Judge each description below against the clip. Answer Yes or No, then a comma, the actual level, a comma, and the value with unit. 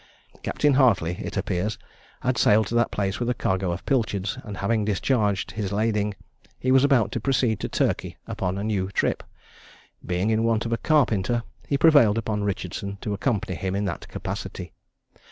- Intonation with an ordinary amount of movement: Yes, average, 3.3 semitones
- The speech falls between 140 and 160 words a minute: No, average, 180 wpm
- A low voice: Yes, low, 105 Hz